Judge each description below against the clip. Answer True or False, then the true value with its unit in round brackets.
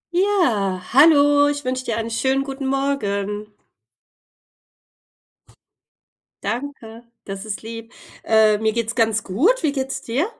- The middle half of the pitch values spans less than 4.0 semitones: False (4.4 semitones)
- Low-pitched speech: False (235 Hz)